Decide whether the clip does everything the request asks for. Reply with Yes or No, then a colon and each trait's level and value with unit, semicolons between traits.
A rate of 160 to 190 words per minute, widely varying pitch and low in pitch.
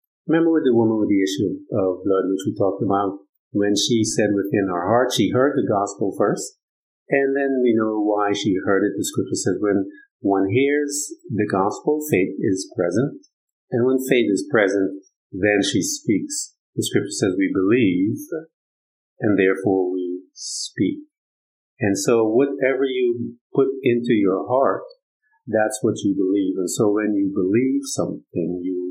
Yes: average, 165 wpm; wide, 6.9 semitones; low, 115 Hz